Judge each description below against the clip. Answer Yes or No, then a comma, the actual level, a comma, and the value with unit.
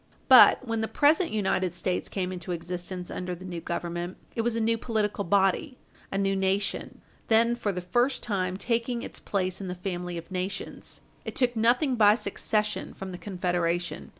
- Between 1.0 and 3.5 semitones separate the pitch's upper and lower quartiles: No, average, 4.0 semitones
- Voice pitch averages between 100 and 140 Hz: No, high, 195 Hz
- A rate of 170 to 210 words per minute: Yes, average, 180 wpm